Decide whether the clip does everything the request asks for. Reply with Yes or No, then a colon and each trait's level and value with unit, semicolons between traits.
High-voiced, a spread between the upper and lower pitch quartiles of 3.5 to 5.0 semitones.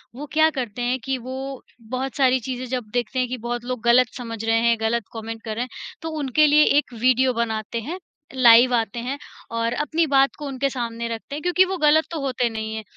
No: very high, 250 Hz; average, 2.8 semitones